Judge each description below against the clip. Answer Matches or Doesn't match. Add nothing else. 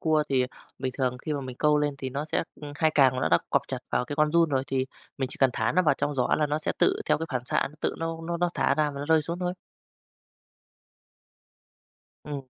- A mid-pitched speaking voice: Matches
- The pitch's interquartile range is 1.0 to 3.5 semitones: Matches